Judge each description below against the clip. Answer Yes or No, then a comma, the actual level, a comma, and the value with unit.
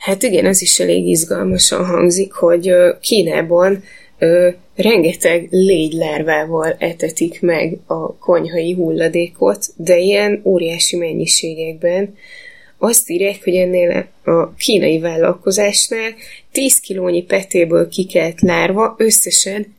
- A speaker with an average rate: No, slow, 100 wpm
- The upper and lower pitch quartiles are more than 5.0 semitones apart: No, average, 2.8 semitones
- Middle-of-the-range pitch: Yes, medium, 180 Hz